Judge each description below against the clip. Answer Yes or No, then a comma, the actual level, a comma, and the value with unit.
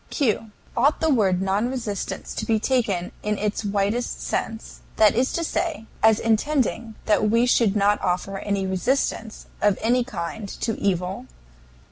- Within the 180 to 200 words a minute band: No, average, 155 wpm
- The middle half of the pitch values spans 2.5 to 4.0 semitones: Yes, average, 3.4 semitones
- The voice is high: Yes, high, 215 Hz